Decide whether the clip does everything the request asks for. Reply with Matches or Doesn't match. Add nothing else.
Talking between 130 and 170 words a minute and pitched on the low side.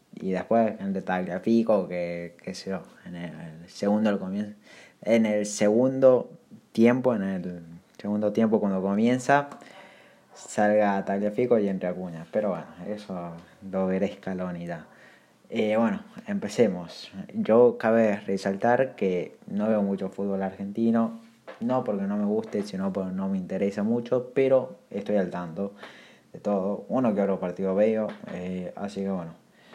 Matches